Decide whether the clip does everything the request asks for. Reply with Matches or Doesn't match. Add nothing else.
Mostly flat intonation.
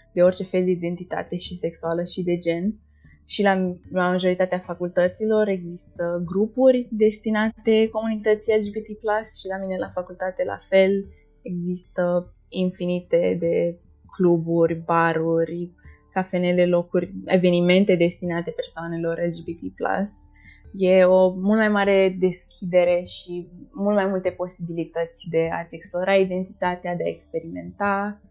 Matches